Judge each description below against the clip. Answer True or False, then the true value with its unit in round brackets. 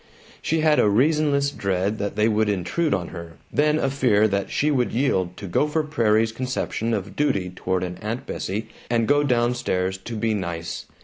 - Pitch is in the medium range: False (110 Hz)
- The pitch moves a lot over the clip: True (6.4 semitones)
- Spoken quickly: False (190 wpm)